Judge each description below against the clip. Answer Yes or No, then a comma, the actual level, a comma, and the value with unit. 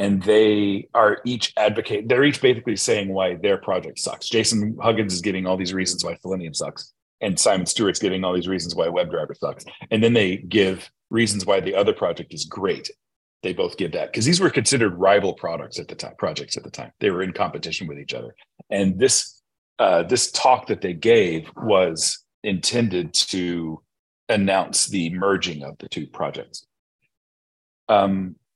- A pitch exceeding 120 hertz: No, very low, 95 Hz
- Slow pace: No, average, 185 wpm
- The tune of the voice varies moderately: Yes, average, 3.6 semitones